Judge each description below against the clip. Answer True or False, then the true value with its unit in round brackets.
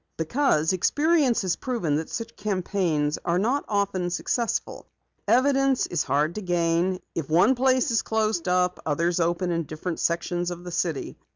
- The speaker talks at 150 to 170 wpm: True (160 wpm)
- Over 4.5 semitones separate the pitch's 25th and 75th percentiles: True (5.2 semitones)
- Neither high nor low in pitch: True (180 Hz)